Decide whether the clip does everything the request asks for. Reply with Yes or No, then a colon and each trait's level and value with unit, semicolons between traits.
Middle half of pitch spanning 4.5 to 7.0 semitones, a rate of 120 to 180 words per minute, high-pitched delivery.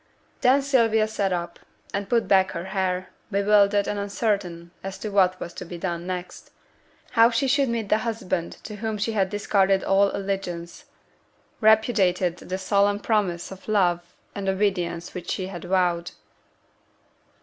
No: average, 2.8 semitones; average, 155 wpm; high, 195 Hz